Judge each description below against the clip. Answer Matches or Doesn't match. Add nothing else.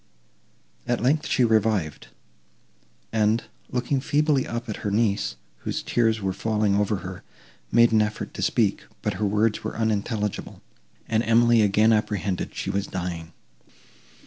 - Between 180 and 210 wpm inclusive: Doesn't match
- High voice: Doesn't match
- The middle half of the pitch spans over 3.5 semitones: Doesn't match